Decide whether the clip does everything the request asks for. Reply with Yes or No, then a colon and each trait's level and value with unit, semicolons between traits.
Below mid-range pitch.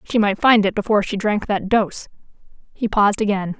No: high, 205 Hz